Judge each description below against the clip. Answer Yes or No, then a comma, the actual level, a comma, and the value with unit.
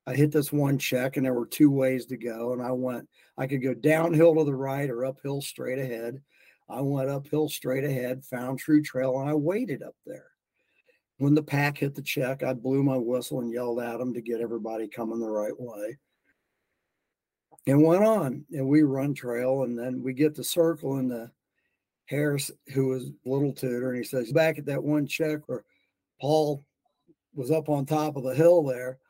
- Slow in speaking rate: No, average, 200 wpm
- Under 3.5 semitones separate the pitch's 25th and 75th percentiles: Yes, average, 2.9 semitones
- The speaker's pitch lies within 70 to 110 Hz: No, low, 135 Hz